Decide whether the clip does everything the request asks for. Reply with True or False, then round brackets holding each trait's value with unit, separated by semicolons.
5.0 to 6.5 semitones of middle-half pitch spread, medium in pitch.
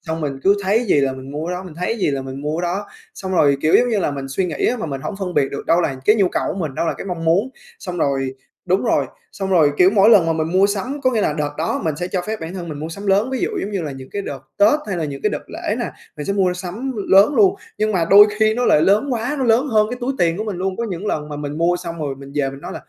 True (5.4 semitones; 180 Hz)